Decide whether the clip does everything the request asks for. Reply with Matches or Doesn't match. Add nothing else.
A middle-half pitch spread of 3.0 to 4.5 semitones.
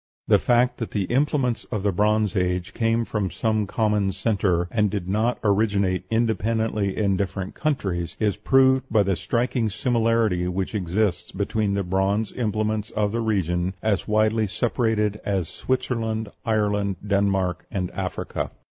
Doesn't match